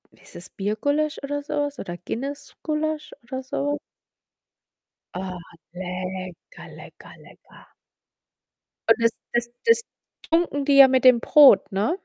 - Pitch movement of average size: No, wide, 6.6 semitones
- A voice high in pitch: Yes, very high, 265 Hz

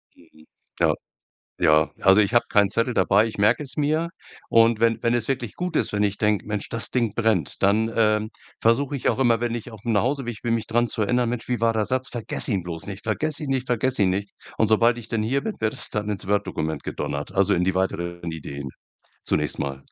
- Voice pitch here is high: No, low, 110 Hz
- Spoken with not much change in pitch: No, average, 3.2 semitones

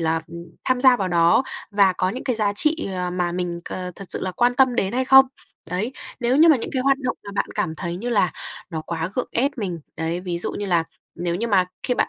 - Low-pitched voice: No, high, 195 Hz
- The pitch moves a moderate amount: No, wide, 6.2 semitones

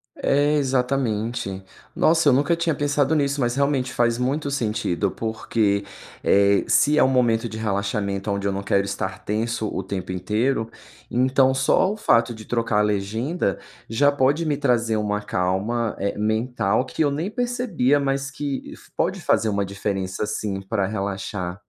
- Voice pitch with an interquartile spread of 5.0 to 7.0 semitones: Yes, wide, 5.4 semitones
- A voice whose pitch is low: Yes, low, 115 Hz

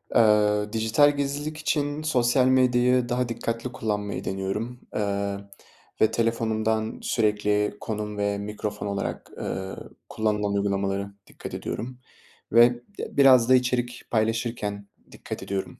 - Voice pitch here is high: No, low, 110 Hz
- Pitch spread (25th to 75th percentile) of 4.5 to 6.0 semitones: No, average, 3.1 semitones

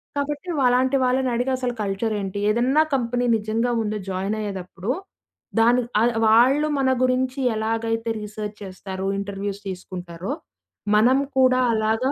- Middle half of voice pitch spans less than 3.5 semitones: No, average, 3.9 semitones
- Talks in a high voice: Yes, high, 225 Hz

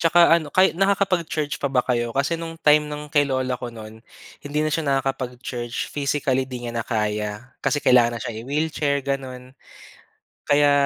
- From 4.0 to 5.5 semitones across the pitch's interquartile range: No, average, 3.5 semitones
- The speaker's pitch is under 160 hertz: Yes, low, 135 Hz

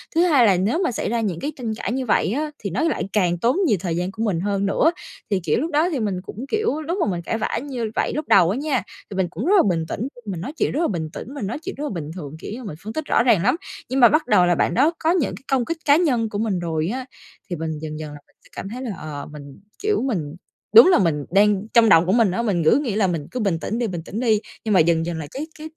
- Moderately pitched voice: No, high, 215 Hz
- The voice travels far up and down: Yes, wide, 7.3 semitones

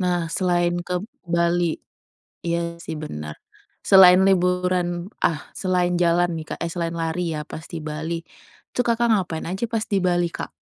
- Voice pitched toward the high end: No, medium, 175 Hz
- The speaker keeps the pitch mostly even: Yes, narrow, 1.4 semitones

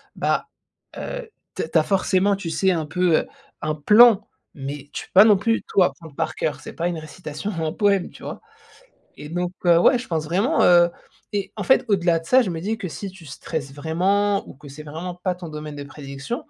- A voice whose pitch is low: No, medium, 175 Hz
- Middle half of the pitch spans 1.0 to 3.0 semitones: No, average, 4.2 semitones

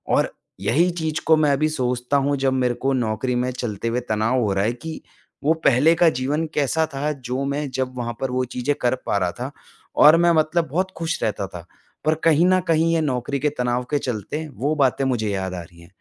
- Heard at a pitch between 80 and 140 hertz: Yes, low, 135 Hz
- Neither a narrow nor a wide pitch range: Yes, average, 4.3 semitones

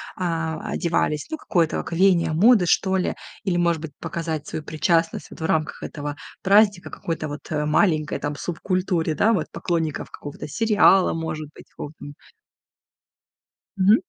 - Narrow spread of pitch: No, average, 3.3 semitones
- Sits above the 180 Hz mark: No, medium, 165 Hz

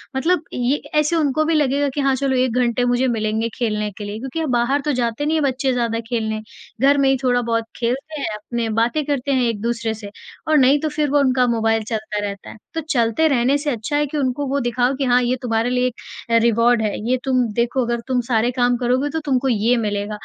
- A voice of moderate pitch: No, very high, 250 Hz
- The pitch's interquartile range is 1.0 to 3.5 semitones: Yes, average, 3.2 semitones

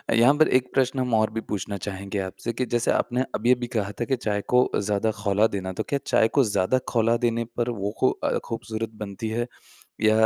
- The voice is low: Yes, low, 110 Hz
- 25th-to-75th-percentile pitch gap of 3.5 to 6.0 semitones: No, average, 2.9 semitones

